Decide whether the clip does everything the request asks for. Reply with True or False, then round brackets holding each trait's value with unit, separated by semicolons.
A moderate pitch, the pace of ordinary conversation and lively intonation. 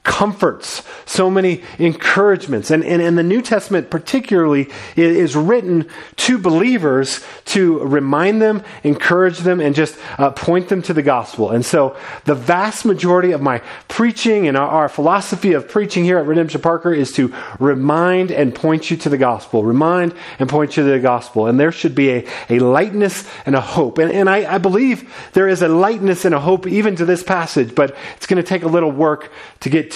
False (170 Hz; 195 wpm; 4.5 semitones)